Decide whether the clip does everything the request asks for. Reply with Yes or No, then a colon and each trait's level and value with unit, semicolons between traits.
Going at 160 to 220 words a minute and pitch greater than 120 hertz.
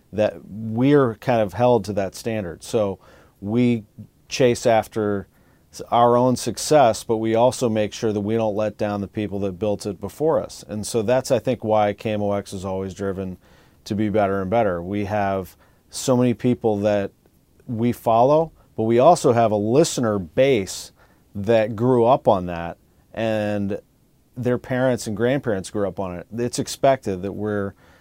No: average, 170 wpm; low, 105 Hz